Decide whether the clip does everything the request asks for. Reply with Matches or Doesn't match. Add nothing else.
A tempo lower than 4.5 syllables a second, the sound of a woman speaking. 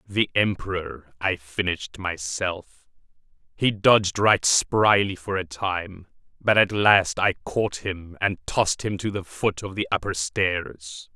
Doesn't match